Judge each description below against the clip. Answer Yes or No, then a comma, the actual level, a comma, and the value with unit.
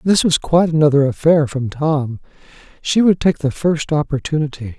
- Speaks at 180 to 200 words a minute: No, average, 165 wpm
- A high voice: No, medium, 150 Hz